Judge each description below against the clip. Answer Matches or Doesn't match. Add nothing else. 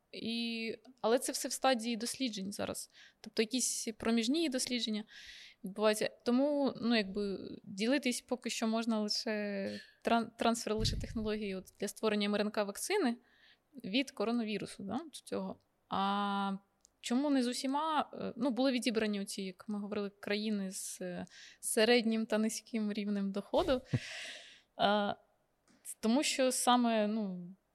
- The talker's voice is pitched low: Doesn't match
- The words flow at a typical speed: Matches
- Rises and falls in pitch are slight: Doesn't match